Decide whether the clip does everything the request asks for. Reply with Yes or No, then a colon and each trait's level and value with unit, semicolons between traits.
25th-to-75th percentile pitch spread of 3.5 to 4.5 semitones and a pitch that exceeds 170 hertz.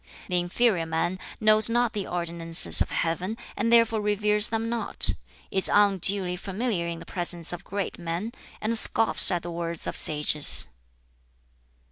Yes: average, 4.1 semitones; high, 190 Hz